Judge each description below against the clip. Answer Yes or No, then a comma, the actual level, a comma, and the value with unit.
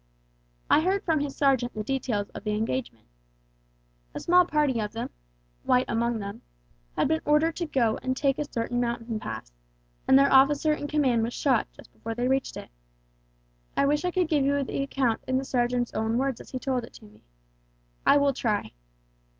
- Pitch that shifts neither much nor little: Yes, average, 3.8 semitones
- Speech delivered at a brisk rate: No, average, 190 wpm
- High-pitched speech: Yes, very high, 260 Hz